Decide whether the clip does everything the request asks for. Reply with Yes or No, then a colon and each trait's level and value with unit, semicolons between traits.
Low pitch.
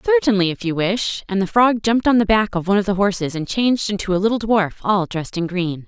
No: high, 200 Hz